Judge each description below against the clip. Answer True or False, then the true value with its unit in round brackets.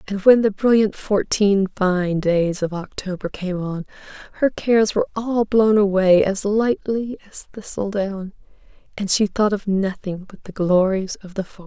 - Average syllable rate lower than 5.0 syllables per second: True (4.5 syllables/s)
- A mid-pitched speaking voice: False (200 Hz)